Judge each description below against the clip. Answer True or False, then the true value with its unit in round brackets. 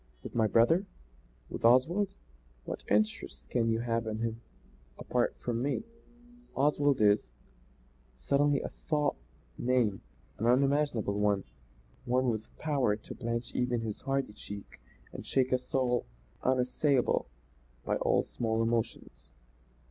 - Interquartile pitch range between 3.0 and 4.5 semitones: True (3.6 semitones)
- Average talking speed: False (130 wpm)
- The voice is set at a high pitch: False (120 Hz)